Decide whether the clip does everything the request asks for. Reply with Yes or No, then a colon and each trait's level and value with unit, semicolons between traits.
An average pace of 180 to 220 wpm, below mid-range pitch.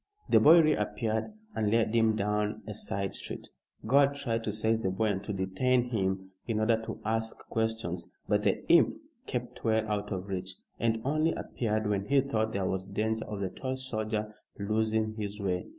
Yes: average, 185 wpm; low, 110 Hz